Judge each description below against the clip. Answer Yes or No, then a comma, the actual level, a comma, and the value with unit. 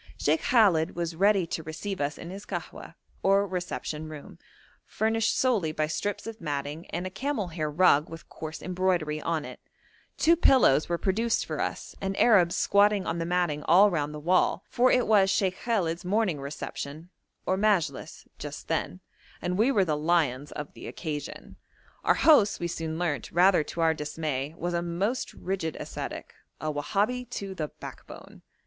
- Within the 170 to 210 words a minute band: Yes, average, 175 wpm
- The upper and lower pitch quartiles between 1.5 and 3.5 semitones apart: No, average, 4.4 semitones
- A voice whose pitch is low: No, medium, 175 Hz